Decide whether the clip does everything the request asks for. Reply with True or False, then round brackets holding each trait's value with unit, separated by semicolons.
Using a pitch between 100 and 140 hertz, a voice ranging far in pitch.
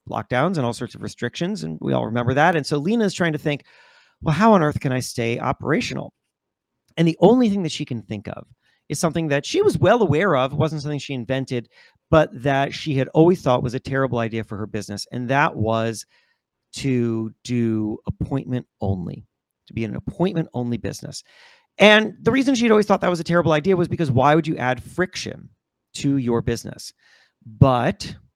True (135 Hz; 6.2 semitones)